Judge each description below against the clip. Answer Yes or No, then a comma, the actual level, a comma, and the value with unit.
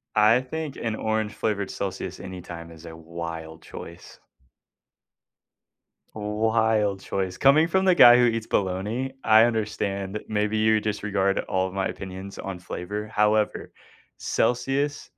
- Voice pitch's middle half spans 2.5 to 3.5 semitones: Yes, average, 3.0 semitones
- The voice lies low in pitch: Yes, low, 105 Hz